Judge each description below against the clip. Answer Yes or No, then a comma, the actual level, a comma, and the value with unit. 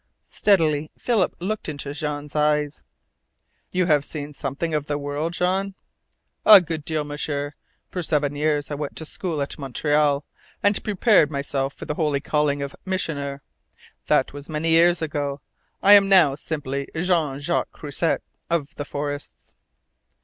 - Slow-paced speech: No, average, 150 wpm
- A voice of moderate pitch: Yes, medium, 150 Hz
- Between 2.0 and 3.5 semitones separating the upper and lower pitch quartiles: Yes, average, 2.8 semitones